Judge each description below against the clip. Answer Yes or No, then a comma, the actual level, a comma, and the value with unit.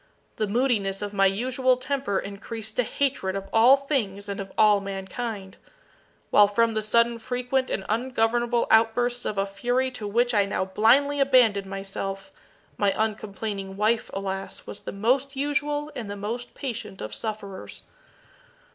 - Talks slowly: No, average, 155 wpm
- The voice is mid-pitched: No, high, 220 Hz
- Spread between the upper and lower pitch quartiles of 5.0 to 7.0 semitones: No, average, 3.9 semitones